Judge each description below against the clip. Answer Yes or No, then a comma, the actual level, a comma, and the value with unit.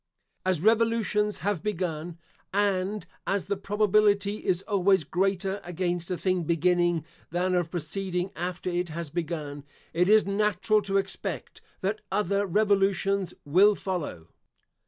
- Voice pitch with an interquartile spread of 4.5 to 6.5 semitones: No, narrow, 2.5 semitones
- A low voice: No, high, 190 Hz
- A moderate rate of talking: No, slow, 130 wpm